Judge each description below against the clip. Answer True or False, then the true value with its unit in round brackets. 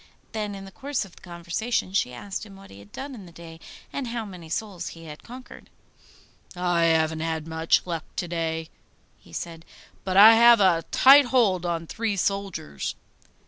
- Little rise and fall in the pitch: False (4.7 semitones)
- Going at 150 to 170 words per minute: False (185 wpm)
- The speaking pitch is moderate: True (180 Hz)